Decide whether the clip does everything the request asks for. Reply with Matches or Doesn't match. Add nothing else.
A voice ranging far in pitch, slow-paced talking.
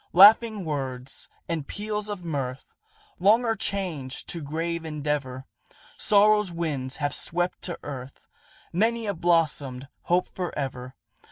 Matches